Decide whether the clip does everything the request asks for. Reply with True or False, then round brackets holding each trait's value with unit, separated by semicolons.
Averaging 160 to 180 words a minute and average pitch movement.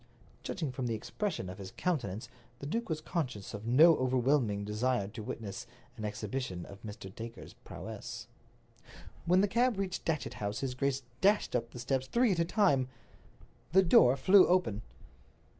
False (165 wpm; 7.8 semitones)